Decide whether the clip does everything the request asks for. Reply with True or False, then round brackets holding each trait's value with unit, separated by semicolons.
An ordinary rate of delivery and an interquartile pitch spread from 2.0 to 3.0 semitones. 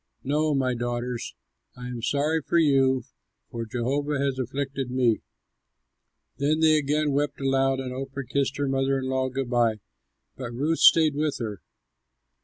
True (155 wpm; 2.4 semitones)